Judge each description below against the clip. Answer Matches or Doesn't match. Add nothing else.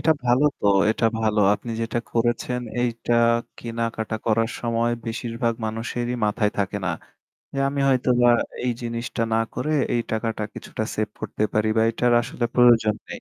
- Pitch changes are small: Matches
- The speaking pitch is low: Matches